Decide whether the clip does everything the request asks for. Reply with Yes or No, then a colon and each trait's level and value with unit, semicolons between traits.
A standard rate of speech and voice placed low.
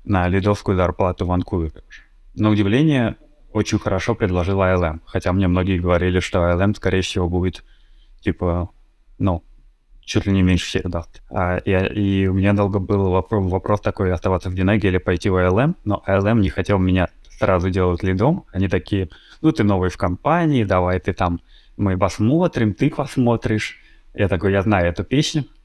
No: fast, 170 wpm; very low, 95 Hz